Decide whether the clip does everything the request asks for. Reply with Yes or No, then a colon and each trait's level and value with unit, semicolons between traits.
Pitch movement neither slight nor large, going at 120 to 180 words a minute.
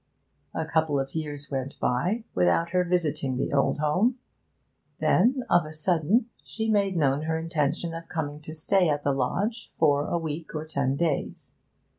Yes: average, 3.2 semitones; average, 170 wpm